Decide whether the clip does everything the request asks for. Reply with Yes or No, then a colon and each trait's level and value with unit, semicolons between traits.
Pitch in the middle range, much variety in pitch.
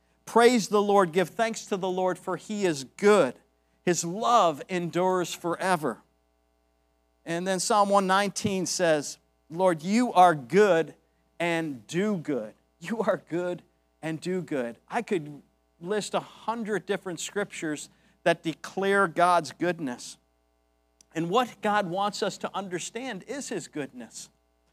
Yes: medium, 180 Hz; wide, 5.8 semitones